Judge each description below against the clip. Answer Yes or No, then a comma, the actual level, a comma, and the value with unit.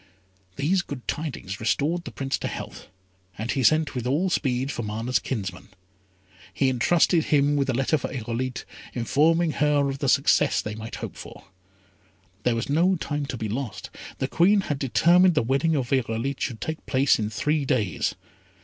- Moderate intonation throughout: Yes, average, 4.5 semitones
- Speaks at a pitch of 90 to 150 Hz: Yes, low, 135 Hz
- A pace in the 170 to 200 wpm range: Yes, average, 175 wpm